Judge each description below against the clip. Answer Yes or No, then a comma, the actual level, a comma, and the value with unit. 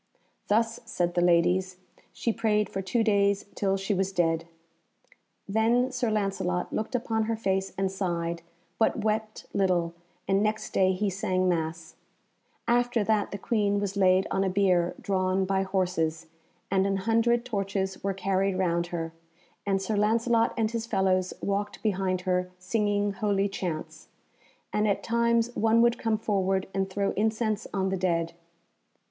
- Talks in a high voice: Yes, high, 195 Hz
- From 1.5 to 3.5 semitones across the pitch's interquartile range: Yes, average, 2.7 semitones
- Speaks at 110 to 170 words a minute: Yes, average, 155 wpm